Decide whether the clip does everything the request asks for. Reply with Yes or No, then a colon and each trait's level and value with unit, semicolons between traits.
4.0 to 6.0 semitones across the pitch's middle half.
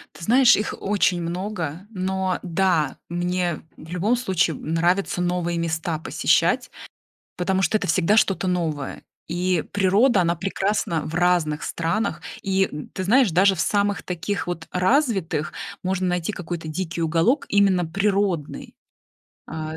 No: average, 2.9 semitones